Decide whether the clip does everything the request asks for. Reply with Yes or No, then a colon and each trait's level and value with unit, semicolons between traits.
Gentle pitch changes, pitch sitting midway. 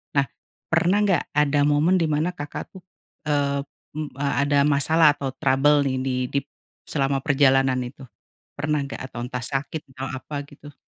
Yes: narrow, 1.7 semitones; medium, 145 Hz